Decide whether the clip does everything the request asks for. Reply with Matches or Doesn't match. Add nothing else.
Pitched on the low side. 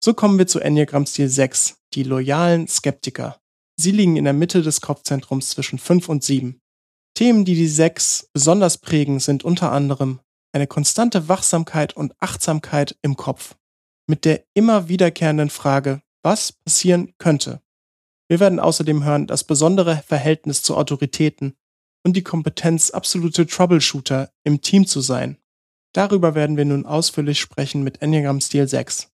Doesn't match